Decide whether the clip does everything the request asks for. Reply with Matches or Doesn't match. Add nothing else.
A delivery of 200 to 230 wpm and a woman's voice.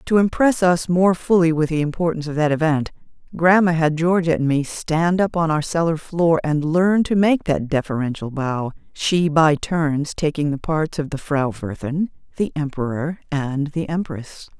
Doesn't match